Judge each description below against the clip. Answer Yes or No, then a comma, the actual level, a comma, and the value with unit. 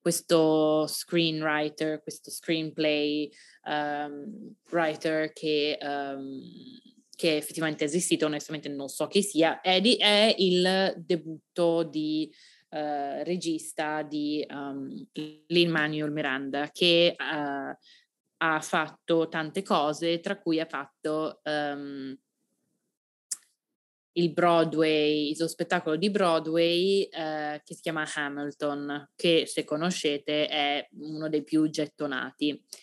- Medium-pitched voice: Yes, medium, 155 Hz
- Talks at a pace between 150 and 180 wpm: No, slow, 115 wpm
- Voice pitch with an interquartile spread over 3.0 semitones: No, narrow, 2.4 semitones